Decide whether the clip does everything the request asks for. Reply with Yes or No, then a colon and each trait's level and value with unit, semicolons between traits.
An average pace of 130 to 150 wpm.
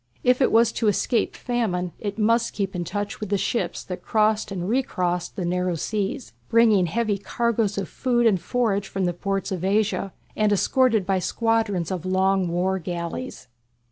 No: average, 175 wpm